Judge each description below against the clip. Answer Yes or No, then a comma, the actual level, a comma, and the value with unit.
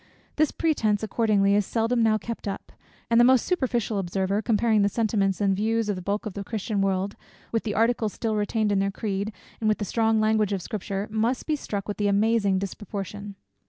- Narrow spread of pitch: Yes, narrow, 2.1 semitones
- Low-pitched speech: No, high, 210 Hz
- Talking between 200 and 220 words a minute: Yes, fast, 205 wpm